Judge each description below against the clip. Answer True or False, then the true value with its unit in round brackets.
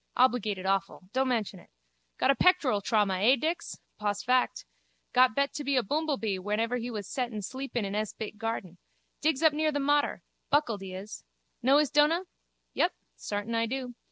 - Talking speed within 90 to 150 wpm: False (180 wpm)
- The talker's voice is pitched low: False (240 Hz)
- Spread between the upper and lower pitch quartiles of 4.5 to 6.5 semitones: True (5.2 semitones)